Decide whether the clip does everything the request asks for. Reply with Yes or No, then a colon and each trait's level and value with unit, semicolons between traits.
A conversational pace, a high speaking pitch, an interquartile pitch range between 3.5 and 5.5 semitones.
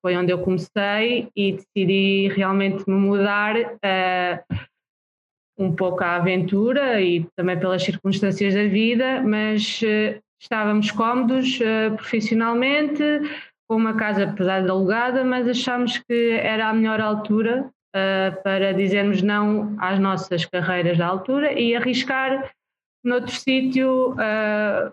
Yes: average, 130 wpm; high, 210 Hz; average, 4.0 semitones